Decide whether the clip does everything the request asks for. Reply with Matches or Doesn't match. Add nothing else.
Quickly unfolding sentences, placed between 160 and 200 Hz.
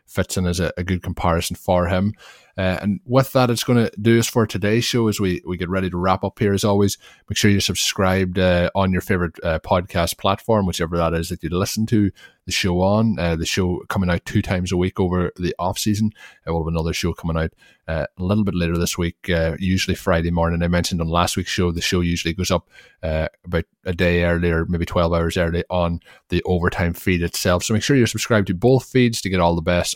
Doesn't match